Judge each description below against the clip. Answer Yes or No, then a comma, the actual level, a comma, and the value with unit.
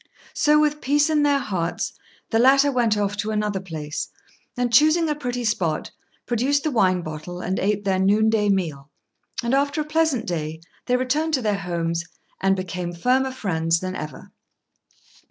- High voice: Yes, high, 215 Hz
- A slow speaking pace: No, average, 170 wpm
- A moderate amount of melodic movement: No, wide, 7.0 semitones